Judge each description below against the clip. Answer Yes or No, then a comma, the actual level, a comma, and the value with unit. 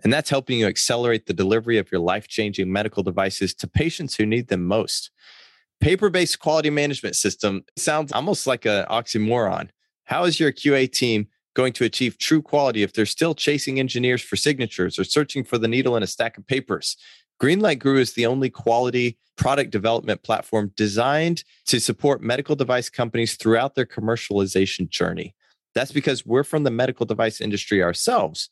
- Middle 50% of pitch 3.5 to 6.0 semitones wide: Yes, average, 4.7 semitones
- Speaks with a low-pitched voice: Yes, low, 120 Hz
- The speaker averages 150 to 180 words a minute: Yes, average, 175 wpm